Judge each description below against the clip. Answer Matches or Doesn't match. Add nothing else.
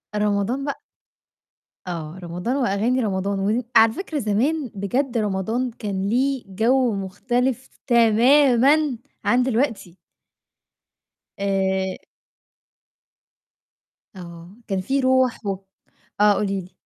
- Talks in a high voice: Matches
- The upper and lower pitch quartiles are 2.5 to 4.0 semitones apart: Doesn't match